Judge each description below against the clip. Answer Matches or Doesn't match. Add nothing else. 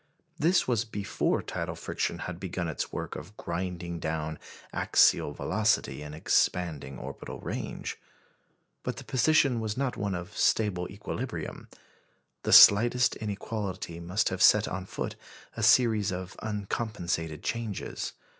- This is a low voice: Matches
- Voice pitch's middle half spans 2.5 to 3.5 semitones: Doesn't match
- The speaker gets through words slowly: Matches